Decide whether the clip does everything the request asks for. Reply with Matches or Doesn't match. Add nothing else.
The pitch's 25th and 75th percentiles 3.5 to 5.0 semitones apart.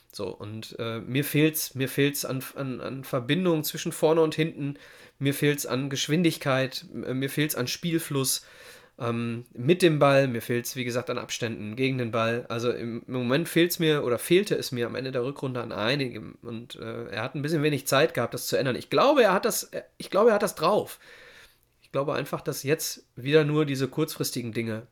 Matches